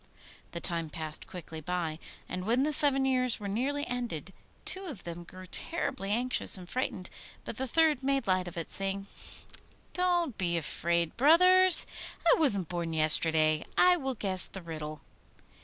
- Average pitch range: No, wide, 7.9 semitones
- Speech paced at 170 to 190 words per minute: No, average, 160 wpm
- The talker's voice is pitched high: Yes, high, 195 Hz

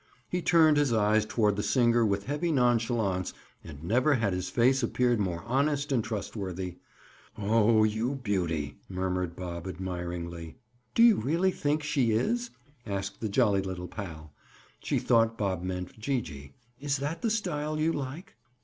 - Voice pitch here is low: Yes, low, 110 Hz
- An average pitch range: No, wide, 6.9 semitones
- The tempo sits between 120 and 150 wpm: No, average, 160 wpm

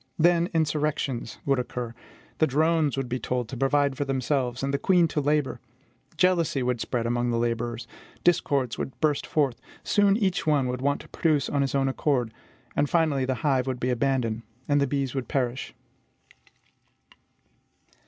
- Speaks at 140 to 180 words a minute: Yes, average, 170 wpm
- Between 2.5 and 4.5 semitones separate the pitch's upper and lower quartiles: Yes, average, 3.3 semitones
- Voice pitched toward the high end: No, low, 135 Hz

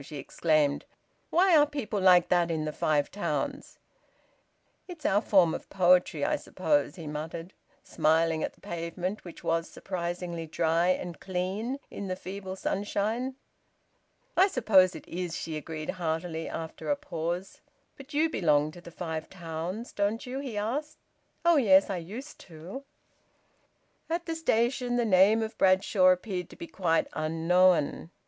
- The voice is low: No, medium, 185 Hz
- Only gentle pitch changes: No, average, 5.1 semitones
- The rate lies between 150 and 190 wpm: Yes, average, 155 wpm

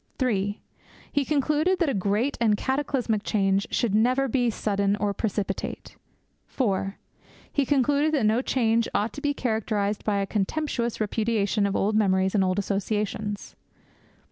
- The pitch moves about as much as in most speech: Yes, average, 4.4 semitones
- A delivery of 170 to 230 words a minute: No, average, 145 wpm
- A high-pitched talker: Yes, high, 215 Hz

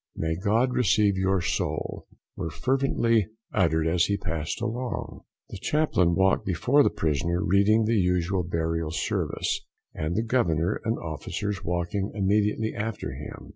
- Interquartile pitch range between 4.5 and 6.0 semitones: Yes, average, 4.8 semitones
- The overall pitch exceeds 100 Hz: No, very low, 95 Hz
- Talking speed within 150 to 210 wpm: No, average, 140 wpm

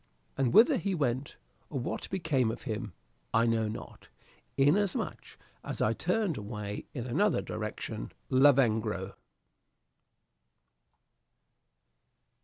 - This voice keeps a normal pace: No, slow, 100 wpm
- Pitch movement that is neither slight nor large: No, wide, 6.1 semitones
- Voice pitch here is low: Yes, low, 125 Hz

